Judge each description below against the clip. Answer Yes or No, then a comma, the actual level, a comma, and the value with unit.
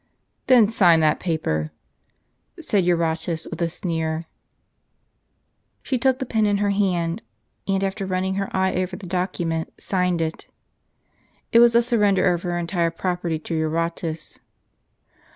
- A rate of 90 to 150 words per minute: Yes, average, 140 wpm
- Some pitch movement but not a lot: Yes, average, 3.1 semitones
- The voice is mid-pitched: Yes, medium, 180 Hz